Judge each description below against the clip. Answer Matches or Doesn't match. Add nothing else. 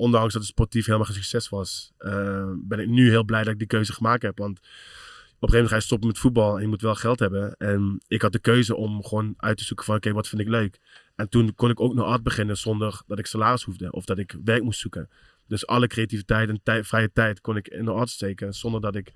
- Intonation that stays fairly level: Matches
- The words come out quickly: Matches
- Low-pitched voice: Matches